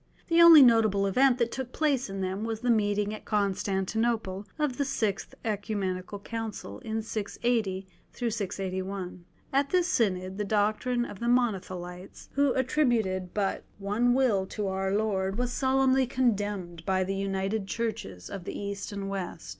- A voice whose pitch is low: No, high, 210 Hz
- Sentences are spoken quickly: No, average, 155 wpm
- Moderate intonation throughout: Yes, average, 3.9 semitones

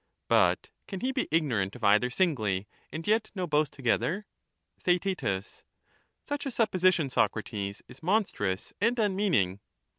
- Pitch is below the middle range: No, medium, 160 Hz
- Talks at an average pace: No, slow, 130 wpm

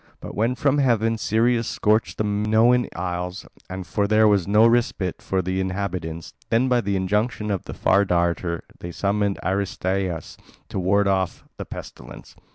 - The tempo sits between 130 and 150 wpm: No, average, 165 wpm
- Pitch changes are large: No, average, 3.0 semitones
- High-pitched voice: No, low, 100 Hz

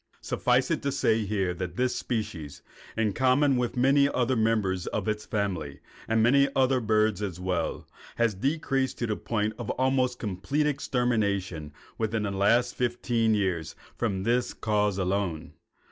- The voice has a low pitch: Yes, low, 110 Hz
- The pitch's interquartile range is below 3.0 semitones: No, average, 4.2 semitones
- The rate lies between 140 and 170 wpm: Yes, average, 155 wpm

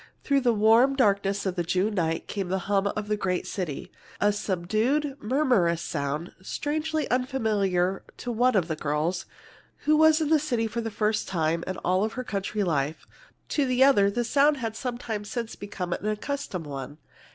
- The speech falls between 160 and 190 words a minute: Yes, average, 185 wpm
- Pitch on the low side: No, high, 210 Hz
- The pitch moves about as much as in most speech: No, wide, 5.7 semitones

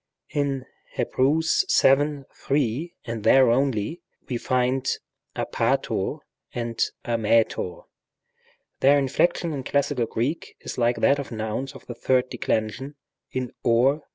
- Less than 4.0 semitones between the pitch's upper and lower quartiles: Yes, average, 3.3 semitones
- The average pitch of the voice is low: Yes, low, 130 Hz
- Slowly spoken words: Yes, slow, 125 wpm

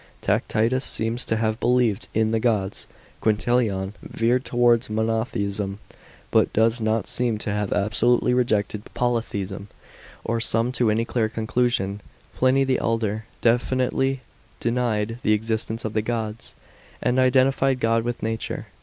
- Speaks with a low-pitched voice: Yes, low, 115 Hz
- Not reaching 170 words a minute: Yes, slow, 135 wpm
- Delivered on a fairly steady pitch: Yes, narrow, 2.3 semitones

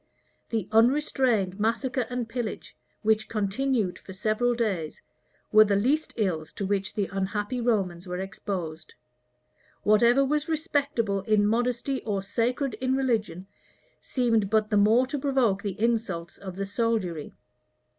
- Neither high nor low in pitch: No, high, 220 Hz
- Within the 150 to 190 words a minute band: No, slow, 135 wpm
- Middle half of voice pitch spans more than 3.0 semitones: Yes, average, 3.9 semitones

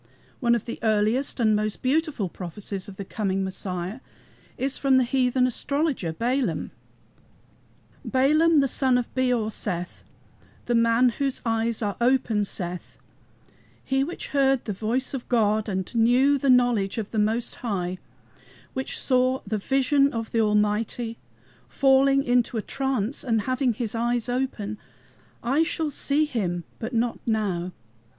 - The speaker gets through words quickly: No, average, 145 wpm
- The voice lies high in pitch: Yes, high, 235 Hz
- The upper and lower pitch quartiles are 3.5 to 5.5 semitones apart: Yes, average, 3.9 semitones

